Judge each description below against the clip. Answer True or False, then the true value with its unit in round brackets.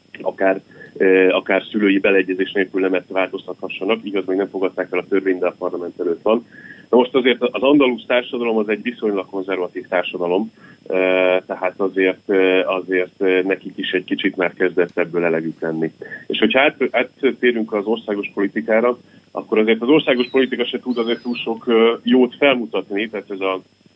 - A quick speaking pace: True (165 wpm)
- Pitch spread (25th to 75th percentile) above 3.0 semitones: True (4.1 semitones)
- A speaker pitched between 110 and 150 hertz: False (100 Hz)